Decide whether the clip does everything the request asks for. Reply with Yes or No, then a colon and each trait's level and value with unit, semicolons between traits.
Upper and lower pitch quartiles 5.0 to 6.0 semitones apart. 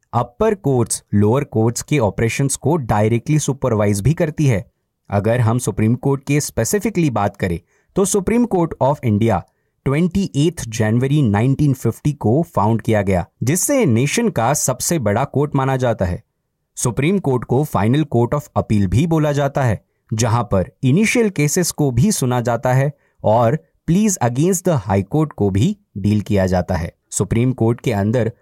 Yes: wide, 5.5 semitones